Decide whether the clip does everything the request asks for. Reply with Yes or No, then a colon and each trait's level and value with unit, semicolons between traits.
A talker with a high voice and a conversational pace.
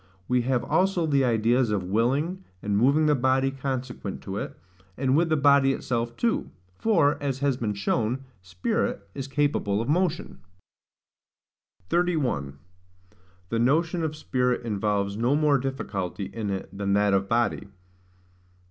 No: low, 130 Hz; average, 145 wpm